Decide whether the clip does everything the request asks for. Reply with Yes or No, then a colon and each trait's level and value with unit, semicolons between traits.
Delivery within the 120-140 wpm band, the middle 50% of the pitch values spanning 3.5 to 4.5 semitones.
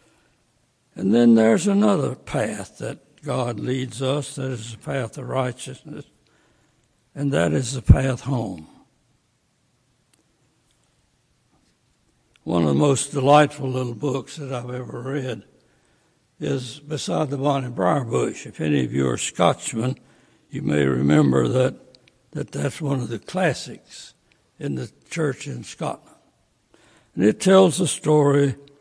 No: slow, 135 wpm; average, 2.8 semitones